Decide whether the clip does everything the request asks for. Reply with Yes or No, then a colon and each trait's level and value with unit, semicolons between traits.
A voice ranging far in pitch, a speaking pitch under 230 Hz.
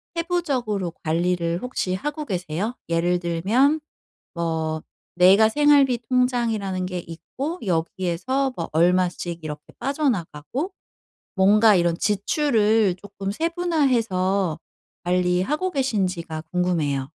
Yes: wide, 6.8 semitones; high, 190 Hz